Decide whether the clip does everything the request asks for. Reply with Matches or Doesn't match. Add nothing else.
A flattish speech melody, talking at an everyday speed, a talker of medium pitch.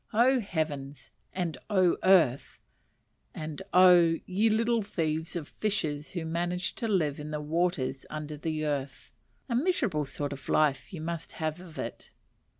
Doesn't match